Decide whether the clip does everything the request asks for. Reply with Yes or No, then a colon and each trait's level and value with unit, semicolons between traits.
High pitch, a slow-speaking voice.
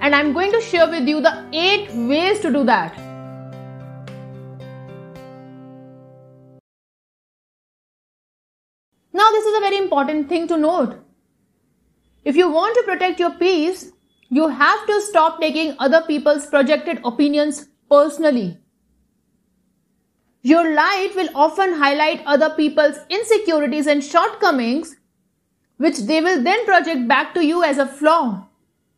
Yes: very high, 295 Hz; slow, 125 wpm